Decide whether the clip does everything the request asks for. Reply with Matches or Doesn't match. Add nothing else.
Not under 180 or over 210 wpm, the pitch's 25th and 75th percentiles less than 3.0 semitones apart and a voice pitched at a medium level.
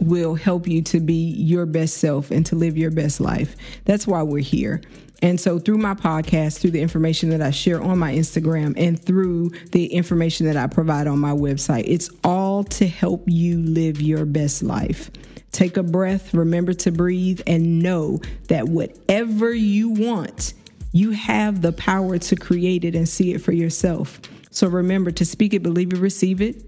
Matches